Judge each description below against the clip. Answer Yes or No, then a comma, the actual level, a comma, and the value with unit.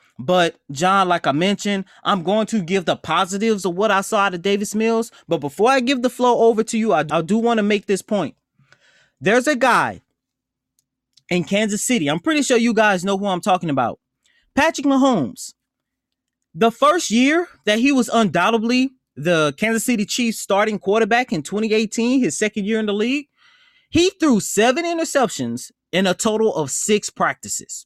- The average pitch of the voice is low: No, high, 215 Hz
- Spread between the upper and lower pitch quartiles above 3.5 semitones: Yes, average, 4.2 semitones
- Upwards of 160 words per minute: Yes, average, 185 wpm